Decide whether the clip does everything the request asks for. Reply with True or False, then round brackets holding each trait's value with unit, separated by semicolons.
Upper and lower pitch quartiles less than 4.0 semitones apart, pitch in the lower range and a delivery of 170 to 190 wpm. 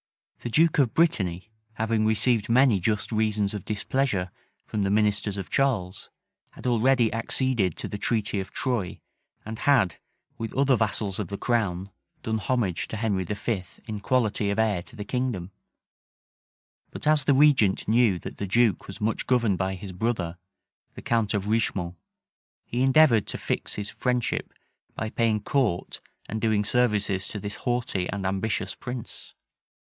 False (3.6 semitones; 110 Hz; 160 wpm)